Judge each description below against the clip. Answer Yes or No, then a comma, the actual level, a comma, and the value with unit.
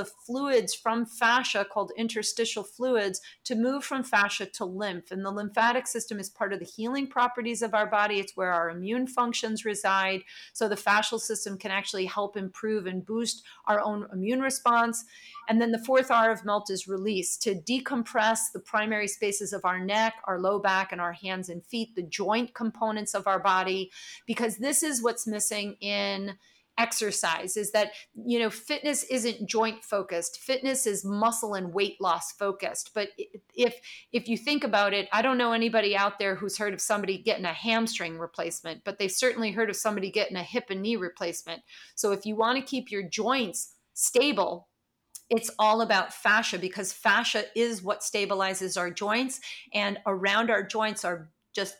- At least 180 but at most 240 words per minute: Yes, average, 185 wpm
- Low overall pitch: No, high, 210 Hz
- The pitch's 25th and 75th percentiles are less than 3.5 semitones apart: Yes, average, 2.8 semitones